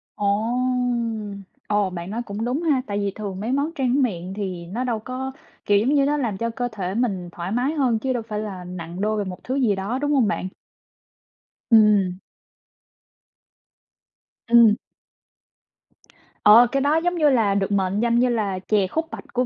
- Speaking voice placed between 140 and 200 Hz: No, high, 215 Hz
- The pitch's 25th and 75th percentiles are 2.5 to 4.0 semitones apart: No, average, 4.4 semitones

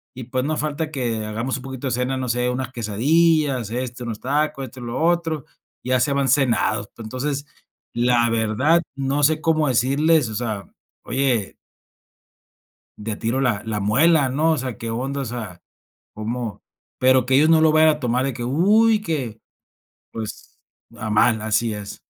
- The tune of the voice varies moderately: Yes, average, 4.2 semitones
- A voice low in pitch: Yes, low, 130 Hz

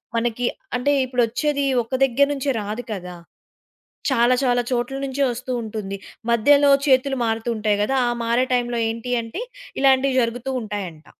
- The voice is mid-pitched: No, high, 240 Hz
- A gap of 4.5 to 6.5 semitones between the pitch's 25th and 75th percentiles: No, average, 3.0 semitones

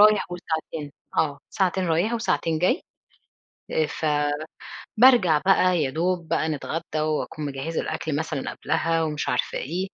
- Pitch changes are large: No, average, 3.0 semitones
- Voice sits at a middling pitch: Yes, medium, 160 Hz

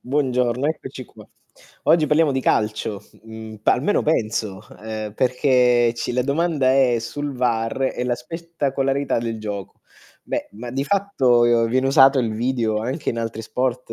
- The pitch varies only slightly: No, average, 3.3 semitones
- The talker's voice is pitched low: Yes, low, 125 Hz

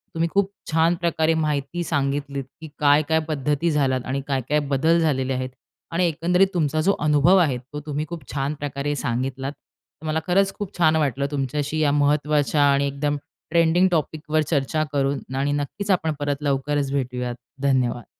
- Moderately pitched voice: Yes, medium, 145 Hz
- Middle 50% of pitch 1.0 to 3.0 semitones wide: Yes, narrow, 2.6 semitones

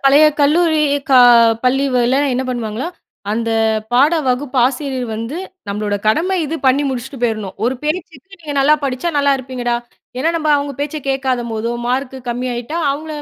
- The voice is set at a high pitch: Yes, very high, 265 Hz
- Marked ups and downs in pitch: No, average, 3.2 semitones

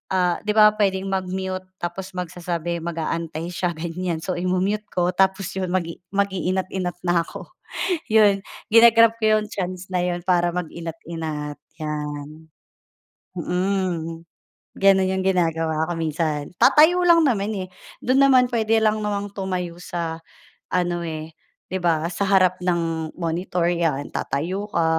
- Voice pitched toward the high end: No, medium, 180 Hz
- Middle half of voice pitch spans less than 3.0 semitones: Yes, narrow, 2.6 semitones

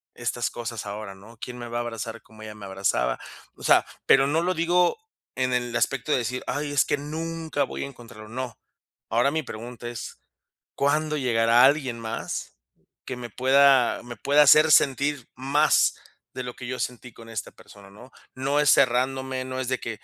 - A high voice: No, low, 125 Hz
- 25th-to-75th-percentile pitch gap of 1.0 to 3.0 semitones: No, average, 3.4 semitones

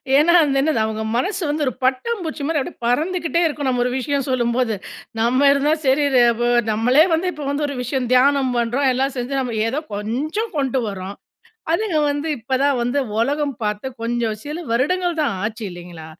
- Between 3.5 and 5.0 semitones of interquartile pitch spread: Yes, average, 4.0 semitones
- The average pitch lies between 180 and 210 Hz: No, very high, 270 Hz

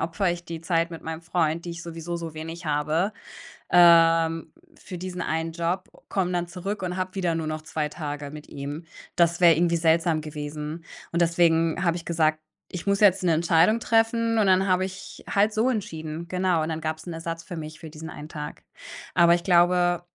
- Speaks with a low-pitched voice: No, medium, 170 Hz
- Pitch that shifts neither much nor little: No, narrow, 2.0 semitones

